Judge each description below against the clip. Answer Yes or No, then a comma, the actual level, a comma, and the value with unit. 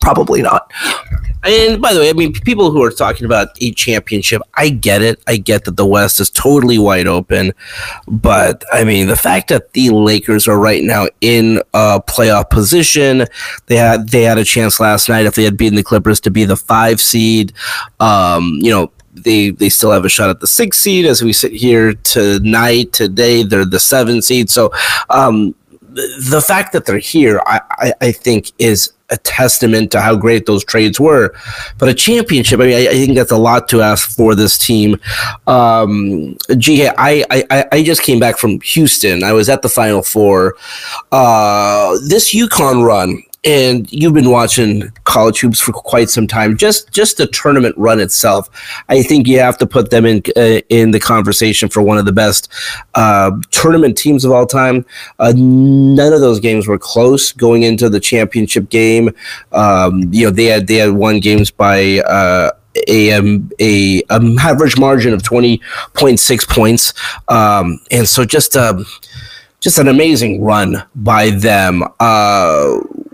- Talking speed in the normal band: Yes, average, 185 wpm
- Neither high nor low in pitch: No, low, 115 Hz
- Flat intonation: No, average, 3.2 semitones